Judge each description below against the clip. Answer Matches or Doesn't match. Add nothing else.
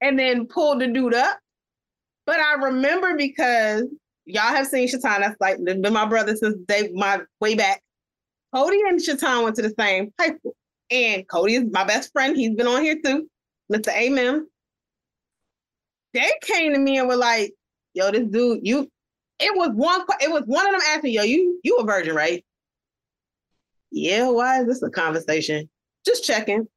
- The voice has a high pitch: Matches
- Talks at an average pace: Matches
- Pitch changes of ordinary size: Doesn't match